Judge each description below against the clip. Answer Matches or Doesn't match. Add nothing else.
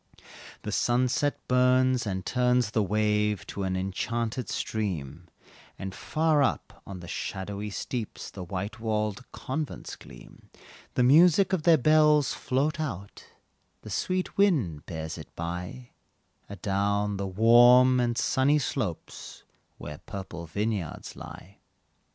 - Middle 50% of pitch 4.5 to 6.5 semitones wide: Matches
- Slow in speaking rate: Matches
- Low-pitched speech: Matches